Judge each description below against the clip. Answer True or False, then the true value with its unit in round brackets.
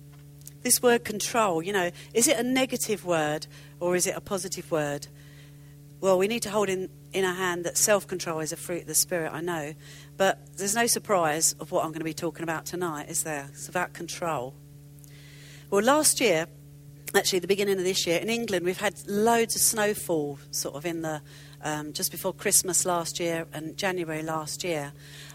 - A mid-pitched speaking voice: True (165 Hz)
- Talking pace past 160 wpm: True (195 wpm)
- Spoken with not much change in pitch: False (4.4 semitones)